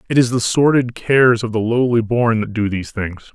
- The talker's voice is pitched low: Yes, low, 115 Hz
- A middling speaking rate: No, fast, 235 wpm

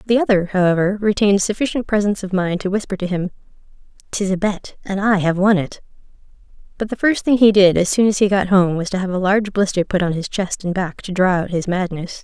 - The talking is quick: Yes, fast, 240 wpm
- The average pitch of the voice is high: Yes, high, 195 Hz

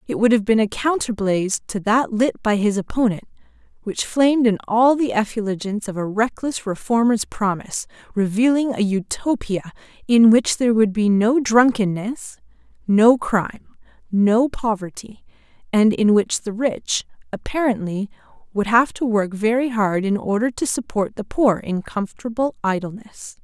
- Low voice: No, high, 220 Hz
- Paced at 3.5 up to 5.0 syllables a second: Yes, 4.7 syllables/s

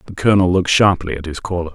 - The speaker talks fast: Yes, fast, 240 wpm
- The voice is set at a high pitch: No, very low, 90 Hz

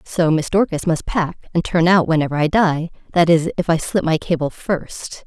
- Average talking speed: No, fast, 215 wpm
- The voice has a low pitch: No, medium, 165 Hz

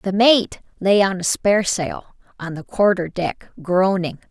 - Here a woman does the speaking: Yes, female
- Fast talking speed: No, average, 155 wpm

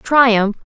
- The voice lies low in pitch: No, high, 235 Hz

